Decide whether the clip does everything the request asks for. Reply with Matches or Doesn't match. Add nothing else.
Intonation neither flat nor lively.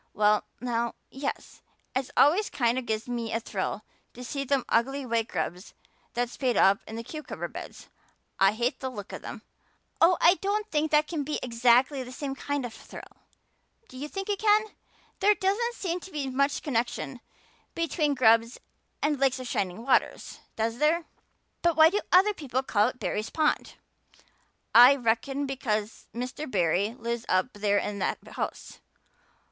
Matches